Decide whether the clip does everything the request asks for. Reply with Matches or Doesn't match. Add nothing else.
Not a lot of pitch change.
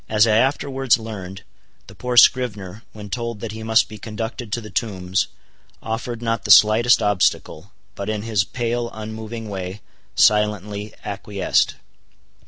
Matches